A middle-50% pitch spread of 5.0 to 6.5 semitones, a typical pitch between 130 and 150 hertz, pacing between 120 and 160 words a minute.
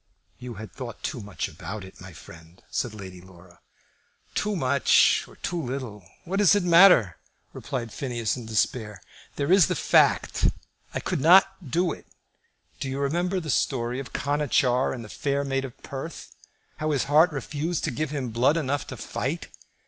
No: wide, 5.5 semitones; low, 135 Hz; average, 175 wpm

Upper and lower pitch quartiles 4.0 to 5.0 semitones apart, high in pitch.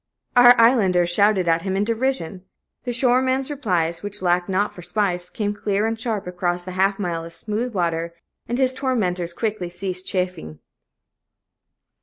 Yes: average, 4.4 semitones; high, 195 Hz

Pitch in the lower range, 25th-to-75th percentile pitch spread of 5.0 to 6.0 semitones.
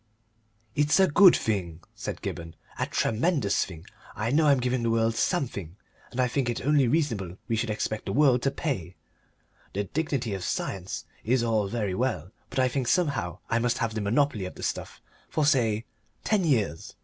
Yes: low, 115 Hz; wide, 5.4 semitones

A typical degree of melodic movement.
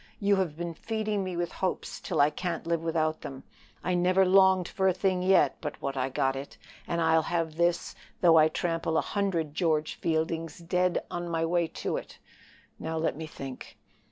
No: narrow, 2.3 semitones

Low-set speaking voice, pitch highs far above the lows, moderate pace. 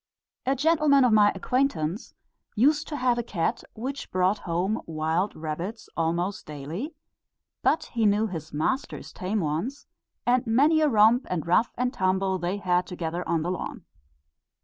No: high, 205 Hz; wide, 6.4 semitones; average, 155 wpm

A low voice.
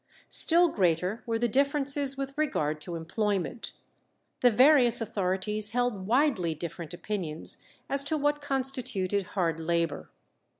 No: high, 215 Hz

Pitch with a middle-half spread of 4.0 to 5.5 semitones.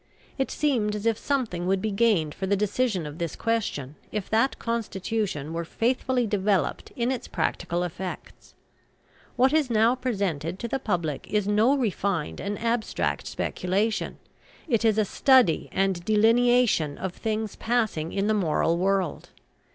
Yes: average, 4.4 semitones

